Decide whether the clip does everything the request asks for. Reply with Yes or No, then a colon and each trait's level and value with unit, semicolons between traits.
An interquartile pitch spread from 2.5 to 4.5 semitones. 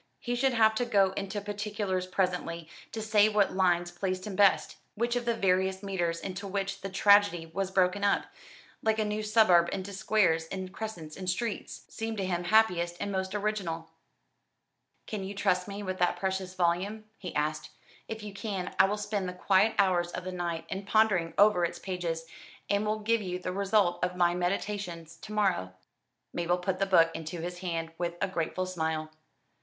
Yes: average, 2.8 semitones